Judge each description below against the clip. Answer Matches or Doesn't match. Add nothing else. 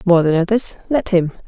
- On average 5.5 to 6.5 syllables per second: Doesn't match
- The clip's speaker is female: Matches